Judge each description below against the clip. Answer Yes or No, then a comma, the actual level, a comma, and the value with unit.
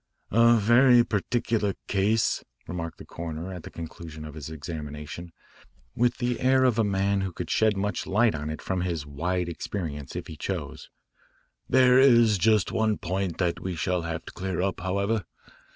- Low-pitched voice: Yes, very low, 95 Hz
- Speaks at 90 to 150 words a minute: No, average, 175 wpm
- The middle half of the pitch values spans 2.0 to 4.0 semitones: No, average, 4.9 semitones